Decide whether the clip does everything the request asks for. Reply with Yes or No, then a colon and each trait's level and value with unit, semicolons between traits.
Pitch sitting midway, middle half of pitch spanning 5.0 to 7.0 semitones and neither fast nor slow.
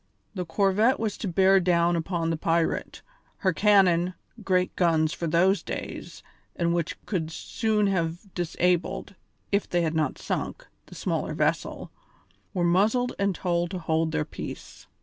No: medium, 175 Hz; average, 2.7 semitones; average, 150 wpm